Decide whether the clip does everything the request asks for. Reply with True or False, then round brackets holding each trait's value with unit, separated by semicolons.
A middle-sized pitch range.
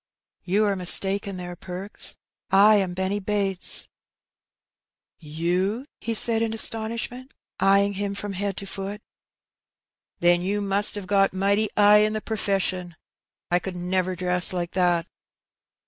False (2.3 semitones)